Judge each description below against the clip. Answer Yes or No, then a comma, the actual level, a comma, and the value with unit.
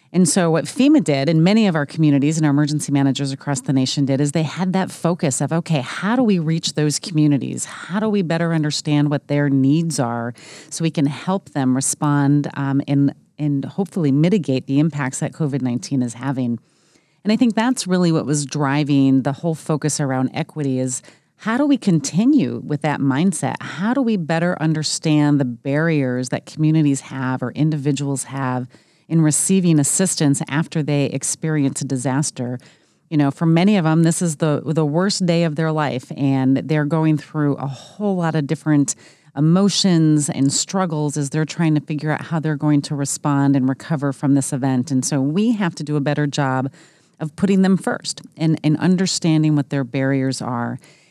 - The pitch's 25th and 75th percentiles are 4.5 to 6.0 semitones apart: No, average, 3.0 semitones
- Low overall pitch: No, medium, 150 Hz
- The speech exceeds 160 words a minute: Yes, average, 190 wpm